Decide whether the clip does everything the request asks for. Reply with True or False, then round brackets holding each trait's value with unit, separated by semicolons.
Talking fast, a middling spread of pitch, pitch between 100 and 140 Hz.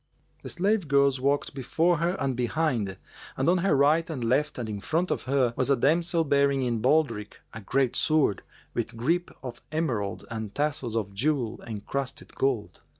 False (175 wpm; 5.0 semitones; 135 Hz)